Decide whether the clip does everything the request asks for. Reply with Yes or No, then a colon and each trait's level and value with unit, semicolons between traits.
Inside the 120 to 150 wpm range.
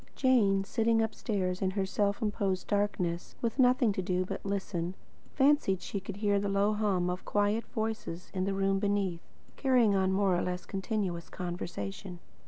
No: average, 175 wpm